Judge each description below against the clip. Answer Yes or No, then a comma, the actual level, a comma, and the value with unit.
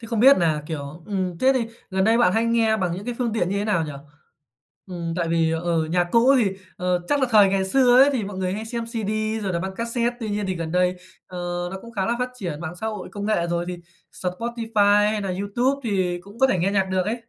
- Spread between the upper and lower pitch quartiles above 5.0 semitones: No, average, 4.3 semitones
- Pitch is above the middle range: Yes, high, 200 Hz